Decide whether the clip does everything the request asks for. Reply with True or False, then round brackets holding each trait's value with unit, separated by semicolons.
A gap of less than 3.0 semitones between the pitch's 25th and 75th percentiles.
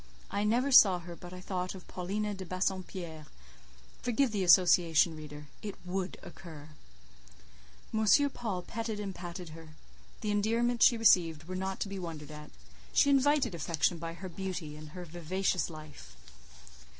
False (3.9 semitones)